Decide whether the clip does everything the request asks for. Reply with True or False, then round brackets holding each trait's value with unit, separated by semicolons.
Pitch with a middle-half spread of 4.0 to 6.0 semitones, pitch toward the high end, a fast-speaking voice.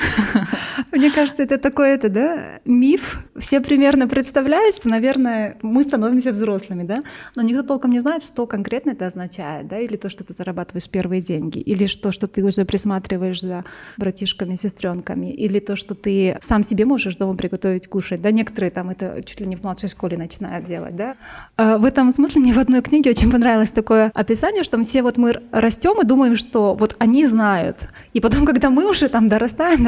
True (5.2 semitones; 225 Hz; 190 wpm)